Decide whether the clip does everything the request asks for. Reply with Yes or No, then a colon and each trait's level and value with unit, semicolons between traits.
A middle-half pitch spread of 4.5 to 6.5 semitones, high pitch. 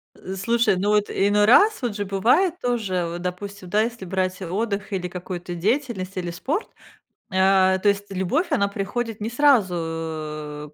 No: average, 3.8 semitones; high, 195 Hz